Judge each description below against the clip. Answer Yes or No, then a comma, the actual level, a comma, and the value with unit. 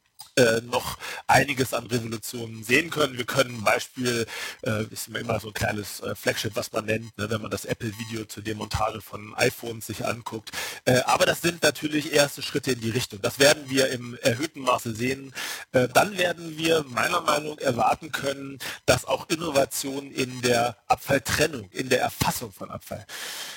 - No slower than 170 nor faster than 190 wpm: Yes, average, 175 wpm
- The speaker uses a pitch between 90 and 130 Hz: Yes, low, 125 Hz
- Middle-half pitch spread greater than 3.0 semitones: Yes, average, 3.8 semitones